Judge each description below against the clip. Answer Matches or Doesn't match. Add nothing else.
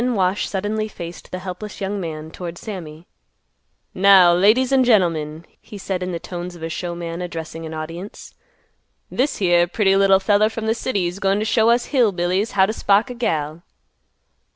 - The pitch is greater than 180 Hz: Matches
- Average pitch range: Matches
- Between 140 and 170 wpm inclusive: Doesn't match